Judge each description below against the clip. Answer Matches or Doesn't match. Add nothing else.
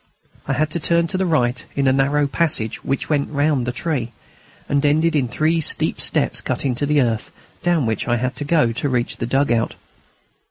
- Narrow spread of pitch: Doesn't match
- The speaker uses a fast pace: Matches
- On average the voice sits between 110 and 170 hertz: Matches